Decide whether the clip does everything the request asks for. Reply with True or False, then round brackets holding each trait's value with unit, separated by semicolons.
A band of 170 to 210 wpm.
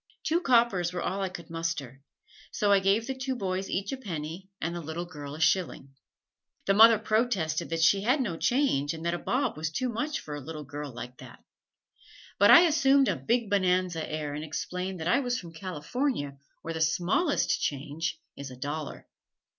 True (195 wpm)